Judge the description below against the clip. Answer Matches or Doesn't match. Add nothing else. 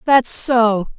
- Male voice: Doesn't match